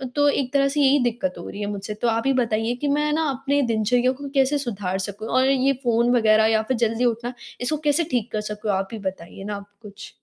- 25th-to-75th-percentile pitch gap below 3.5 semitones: No, average, 4.2 semitones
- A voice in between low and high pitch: No, high, 240 Hz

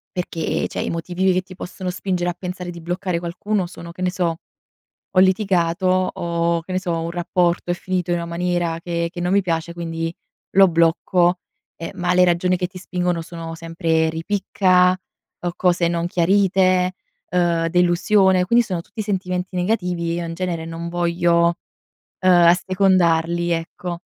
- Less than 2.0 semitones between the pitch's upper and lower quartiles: Yes, narrow, 1.5 semitones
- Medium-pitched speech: Yes, medium, 175 Hz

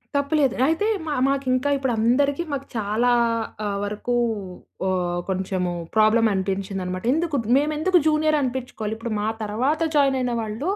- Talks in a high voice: Yes, high, 245 Hz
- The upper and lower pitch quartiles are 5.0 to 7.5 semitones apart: Yes, wide, 5.5 semitones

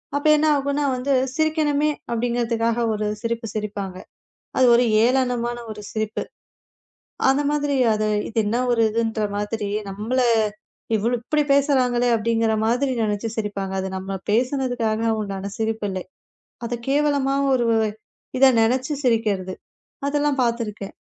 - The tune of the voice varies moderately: Yes, average, 3.8 semitones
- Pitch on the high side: Yes, high, 235 Hz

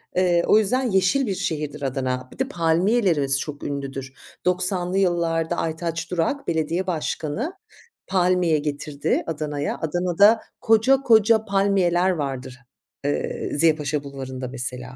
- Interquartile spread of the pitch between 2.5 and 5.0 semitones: Yes, average, 4.7 semitones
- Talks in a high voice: No, medium, 165 Hz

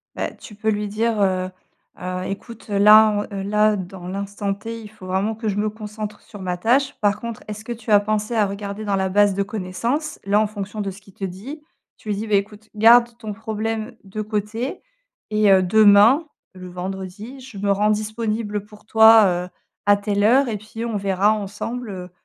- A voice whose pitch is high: Yes, high, 210 Hz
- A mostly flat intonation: Yes, narrow, 1.8 semitones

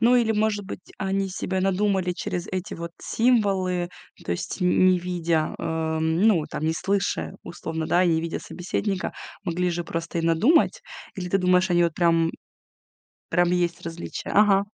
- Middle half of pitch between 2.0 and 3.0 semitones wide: Yes, narrow, 2.6 semitones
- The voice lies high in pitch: No, medium, 180 Hz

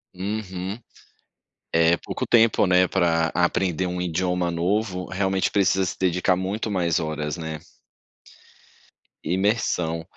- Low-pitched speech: Yes, very low, 90 Hz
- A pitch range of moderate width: No, narrow, 2.1 semitones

